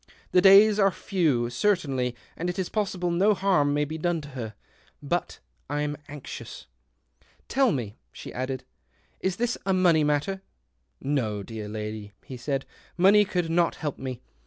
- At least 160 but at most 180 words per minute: Yes, average, 175 wpm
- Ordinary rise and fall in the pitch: No, wide, 6.6 semitones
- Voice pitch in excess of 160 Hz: No, medium, 150 Hz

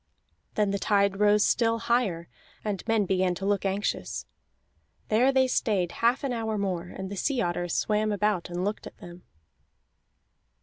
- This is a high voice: Yes, high, 205 Hz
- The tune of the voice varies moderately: Yes, average, 3.1 semitones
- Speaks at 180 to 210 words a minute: No, average, 165 wpm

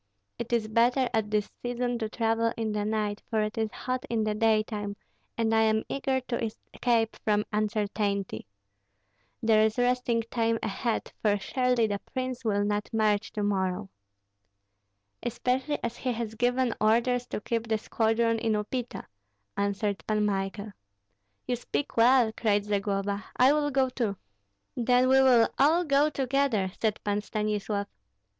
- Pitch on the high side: Yes, high, 225 Hz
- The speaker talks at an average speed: Yes, average, 155 wpm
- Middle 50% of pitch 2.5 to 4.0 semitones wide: Yes, average, 2.8 semitones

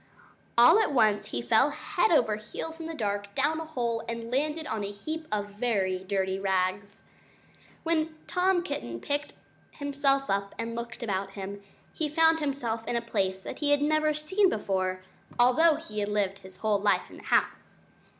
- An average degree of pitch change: No, wide, 7.1 semitones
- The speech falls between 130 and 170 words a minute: No, average, 180 wpm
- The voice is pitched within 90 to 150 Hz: No, high, 235 Hz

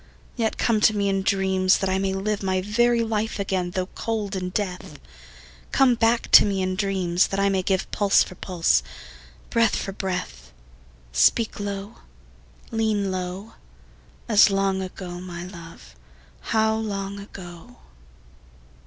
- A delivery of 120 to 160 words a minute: Yes, average, 145 wpm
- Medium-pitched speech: No, high, 195 Hz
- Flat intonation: Yes, narrow, 2.3 semitones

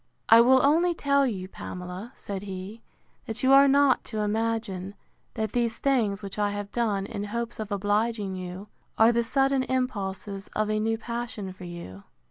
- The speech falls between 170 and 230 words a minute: Yes, average, 175 wpm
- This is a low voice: No, high, 215 Hz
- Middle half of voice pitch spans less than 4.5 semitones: Yes, average, 3.4 semitones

